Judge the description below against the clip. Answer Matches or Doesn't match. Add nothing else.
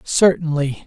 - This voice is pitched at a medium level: Matches